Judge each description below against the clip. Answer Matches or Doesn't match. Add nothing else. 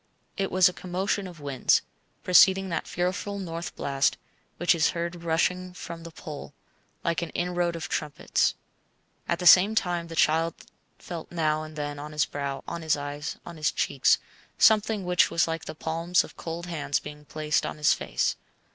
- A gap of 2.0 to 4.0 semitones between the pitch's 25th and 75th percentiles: Matches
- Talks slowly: Doesn't match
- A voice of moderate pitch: Matches